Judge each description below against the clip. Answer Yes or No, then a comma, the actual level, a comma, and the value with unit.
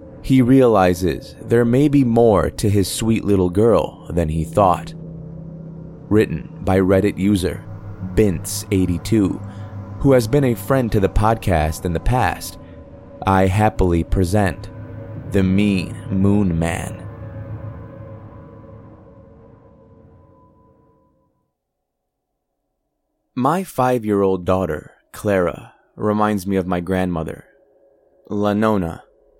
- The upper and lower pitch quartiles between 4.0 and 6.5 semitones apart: No, average, 3.2 semitones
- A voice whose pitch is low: Yes, low, 105 Hz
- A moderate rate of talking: No, slow, 100 wpm